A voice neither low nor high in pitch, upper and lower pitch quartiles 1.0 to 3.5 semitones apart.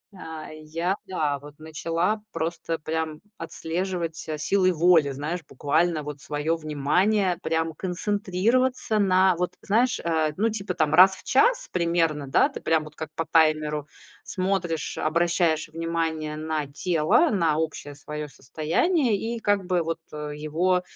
Yes: medium, 165 Hz; average, 3.2 semitones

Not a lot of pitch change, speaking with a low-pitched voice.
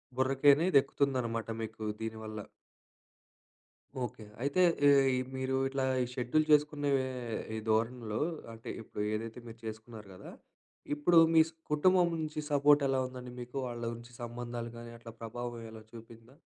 No: average, 3.7 semitones; low, 120 Hz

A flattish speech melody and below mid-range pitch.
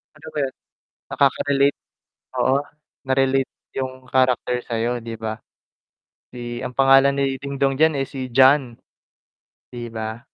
Yes: narrow, 2.2 semitones; low, 130 Hz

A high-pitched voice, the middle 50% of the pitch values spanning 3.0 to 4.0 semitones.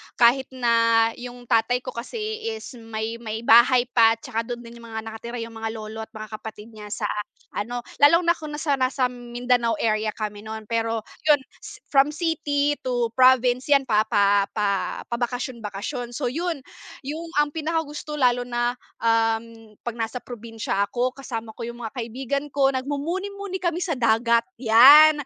Yes: high, 240 Hz; average, 3.7 semitones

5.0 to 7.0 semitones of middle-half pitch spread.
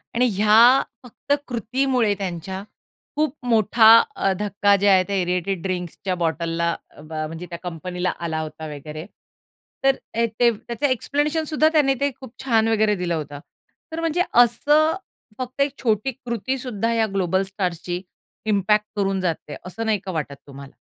Yes: wide, 5.6 semitones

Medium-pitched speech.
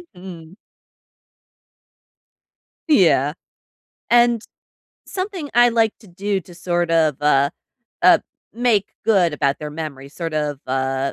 Yes: medium, 170 Hz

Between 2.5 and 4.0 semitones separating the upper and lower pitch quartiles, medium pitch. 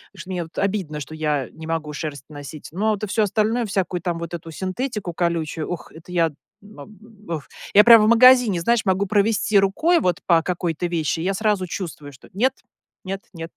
No: average, 4.4 semitones; medium, 180 Hz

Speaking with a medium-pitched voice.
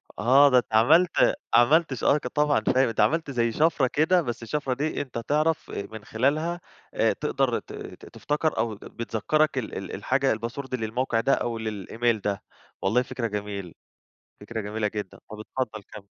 No: low, 120 Hz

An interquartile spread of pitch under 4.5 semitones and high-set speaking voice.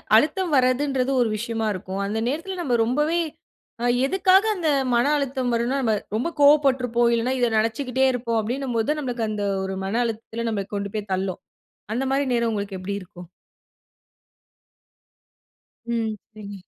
Yes: average, 4.0 semitones; high, 235 Hz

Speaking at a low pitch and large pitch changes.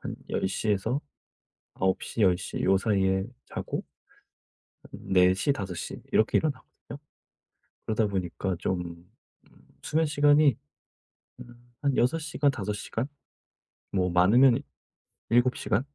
Yes: low, 105 Hz; wide, 5.7 semitones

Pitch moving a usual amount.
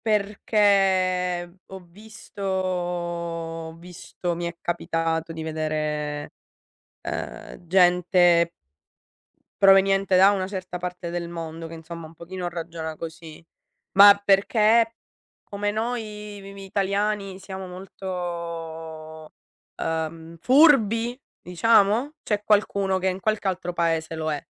Yes: average, 3.1 semitones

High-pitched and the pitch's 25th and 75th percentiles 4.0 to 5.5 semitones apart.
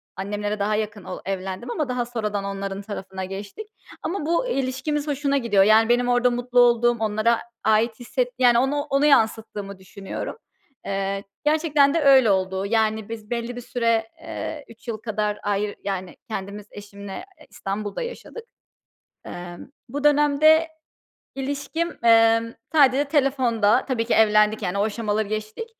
Yes: high, 225 Hz; average, 4.7 semitones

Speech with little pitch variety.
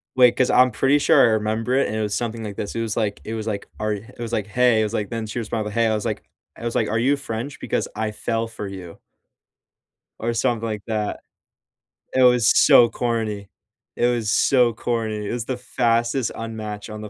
Yes: narrow, 1.9 semitones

